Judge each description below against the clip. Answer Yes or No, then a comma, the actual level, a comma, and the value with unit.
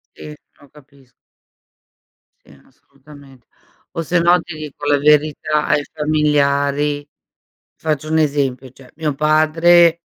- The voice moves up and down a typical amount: No, narrow, 1.7 semitones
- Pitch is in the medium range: Yes, medium, 150 Hz